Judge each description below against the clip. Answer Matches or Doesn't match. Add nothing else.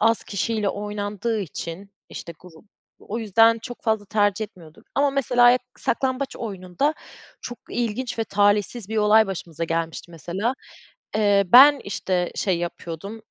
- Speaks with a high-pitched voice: Matches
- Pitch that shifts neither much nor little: Matches